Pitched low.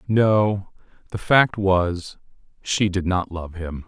Yes: very low, 95 Hz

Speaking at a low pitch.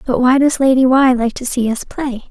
No: very high, 255 Hz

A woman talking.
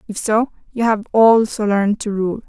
Yes: female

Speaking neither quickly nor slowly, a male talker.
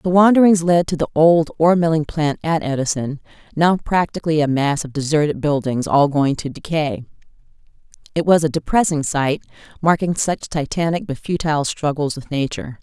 No: average, 165 wpm; female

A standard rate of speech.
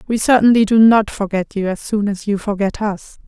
No: fast, 220 wpm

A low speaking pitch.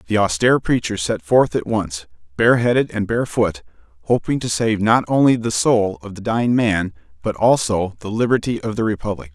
Yes: low, 105 Hz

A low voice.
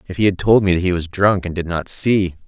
Yes: very low, 90 Hz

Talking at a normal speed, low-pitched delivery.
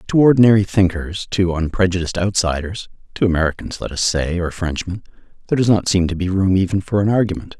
Yes: average, 175 wpm; very low, 95 Hz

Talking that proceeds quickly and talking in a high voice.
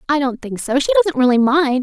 Yes: fast, 230 wpm; very high, 280 Hz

